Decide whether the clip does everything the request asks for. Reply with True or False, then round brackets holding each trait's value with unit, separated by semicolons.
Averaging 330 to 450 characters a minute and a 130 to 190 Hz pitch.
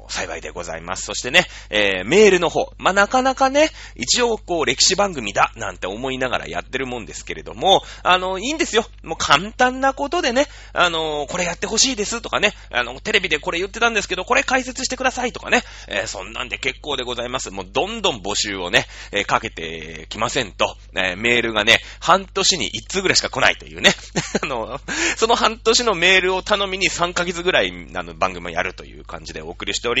True (430 characters per minute; 185 Hz)